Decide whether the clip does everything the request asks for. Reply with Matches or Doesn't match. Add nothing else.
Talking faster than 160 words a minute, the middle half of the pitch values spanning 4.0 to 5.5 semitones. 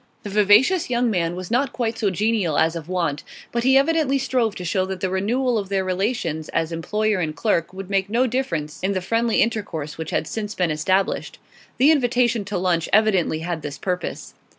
Matches